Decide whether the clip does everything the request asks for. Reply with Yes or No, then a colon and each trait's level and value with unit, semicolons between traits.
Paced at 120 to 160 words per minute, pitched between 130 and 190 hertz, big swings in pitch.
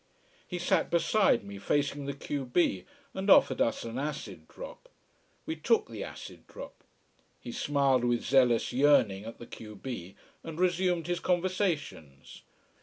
Yes: average, 150 wpm; medium, 140 Hz; wide, 6.8 semitones